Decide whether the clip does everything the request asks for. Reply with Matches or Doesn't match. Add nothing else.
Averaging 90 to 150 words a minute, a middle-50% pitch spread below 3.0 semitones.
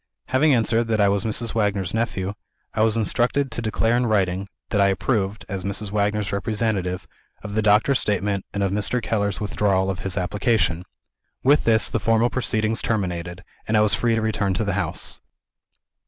Doesn't match